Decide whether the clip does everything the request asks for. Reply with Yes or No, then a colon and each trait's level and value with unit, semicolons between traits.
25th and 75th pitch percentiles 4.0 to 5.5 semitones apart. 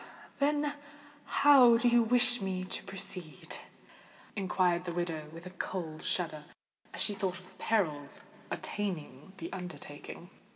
Yes: average, 4.9 semitones